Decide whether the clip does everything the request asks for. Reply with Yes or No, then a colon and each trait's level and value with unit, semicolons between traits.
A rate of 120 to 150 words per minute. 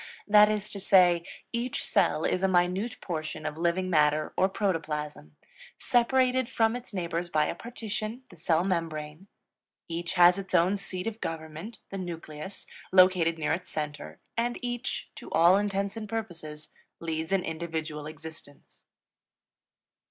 Yes: average, 145 wpm